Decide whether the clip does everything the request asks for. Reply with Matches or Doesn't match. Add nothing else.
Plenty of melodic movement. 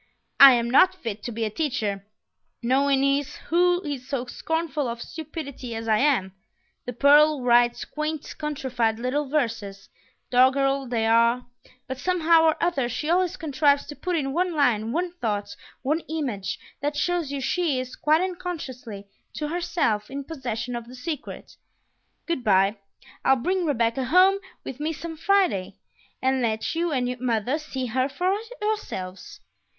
Doesn't match